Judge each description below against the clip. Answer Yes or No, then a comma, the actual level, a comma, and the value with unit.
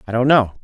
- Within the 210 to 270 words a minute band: No, fast, 285 wpm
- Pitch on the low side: Yes, low, 120 Hz